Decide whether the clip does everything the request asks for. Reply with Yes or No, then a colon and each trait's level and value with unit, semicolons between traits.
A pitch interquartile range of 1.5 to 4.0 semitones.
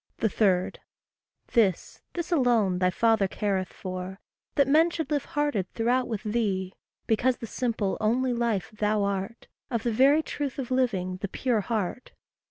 No: average, 4.7 semitones